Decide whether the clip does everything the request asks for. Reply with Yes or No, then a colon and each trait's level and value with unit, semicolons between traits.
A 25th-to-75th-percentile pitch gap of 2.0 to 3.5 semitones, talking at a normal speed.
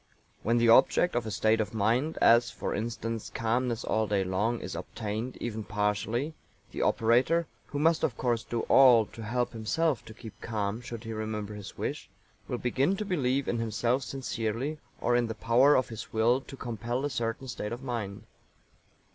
Yes: narrow, 2.5 semitones; average, 185 wpm